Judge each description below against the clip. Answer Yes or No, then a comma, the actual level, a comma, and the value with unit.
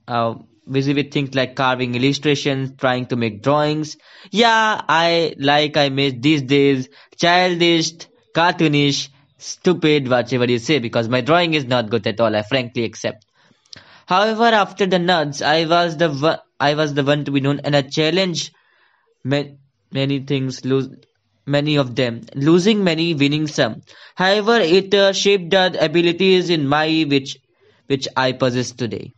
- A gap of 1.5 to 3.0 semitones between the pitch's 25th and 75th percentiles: No, average, 4.0 semitones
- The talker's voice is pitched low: No, medium, 145 Hz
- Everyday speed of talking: Yes, average, 155 wpm